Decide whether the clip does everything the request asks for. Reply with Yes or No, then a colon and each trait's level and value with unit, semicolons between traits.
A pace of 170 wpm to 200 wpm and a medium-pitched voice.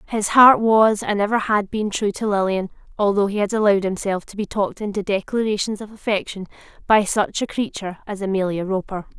No: average, 190 wpm; high, 205 Hz